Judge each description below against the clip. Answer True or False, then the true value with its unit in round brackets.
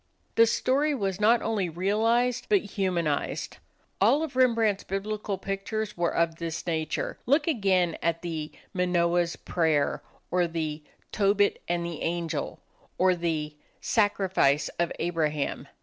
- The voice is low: False (180 Hz)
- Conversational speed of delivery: False (130 wpm)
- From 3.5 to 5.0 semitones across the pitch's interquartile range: True (4.3 semitones)